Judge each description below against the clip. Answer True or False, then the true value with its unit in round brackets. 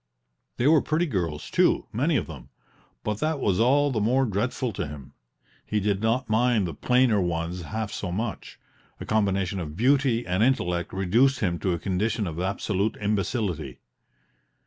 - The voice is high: False (105 Hz)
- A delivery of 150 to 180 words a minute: True (170 wpm)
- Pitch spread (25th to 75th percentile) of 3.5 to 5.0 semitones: False (5.4 semitones)